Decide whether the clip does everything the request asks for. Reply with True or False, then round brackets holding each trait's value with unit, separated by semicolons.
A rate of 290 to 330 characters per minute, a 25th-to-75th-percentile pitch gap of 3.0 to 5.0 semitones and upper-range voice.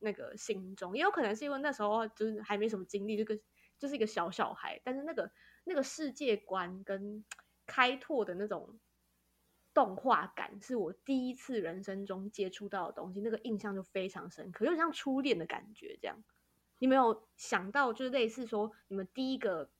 True (295 characters per minute; 4.7 semitones; 220 Hz)